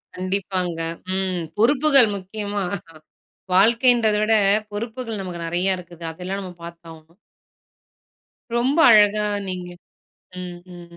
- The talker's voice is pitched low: No, high, 190 Hz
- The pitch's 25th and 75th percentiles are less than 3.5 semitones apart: No, average, 3.8 semitones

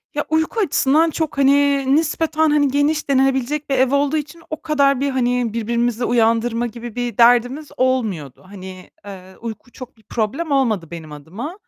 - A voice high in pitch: Yes, very high, 255 Hz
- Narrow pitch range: No, average, 4.2 semitones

